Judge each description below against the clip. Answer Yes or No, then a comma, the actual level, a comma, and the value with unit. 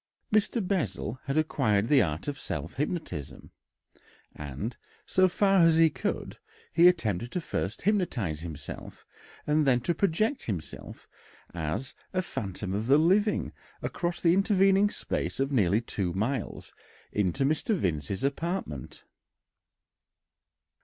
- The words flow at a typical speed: No, slow, 125 wpm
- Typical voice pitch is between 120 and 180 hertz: Yes, low, 135 Hz